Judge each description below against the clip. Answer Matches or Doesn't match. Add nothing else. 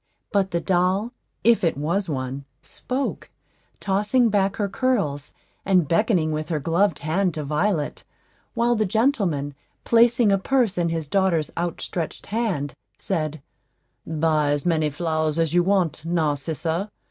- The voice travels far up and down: Doesn't match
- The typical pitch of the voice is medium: Matches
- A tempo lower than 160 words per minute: Matches